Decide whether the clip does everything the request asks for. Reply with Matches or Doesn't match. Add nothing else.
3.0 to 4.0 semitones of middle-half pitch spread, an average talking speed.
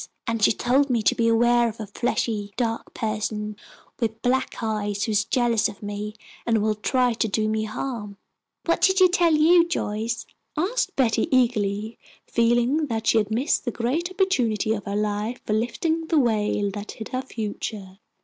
Matches